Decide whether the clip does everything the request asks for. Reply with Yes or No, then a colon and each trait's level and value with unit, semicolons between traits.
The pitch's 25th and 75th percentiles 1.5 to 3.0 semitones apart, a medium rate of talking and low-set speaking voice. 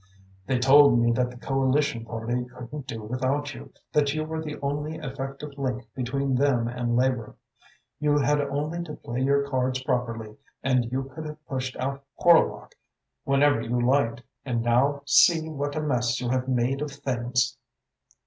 Yes: average, 2.7 semitones; average, 170 wpm; low, 130 Hz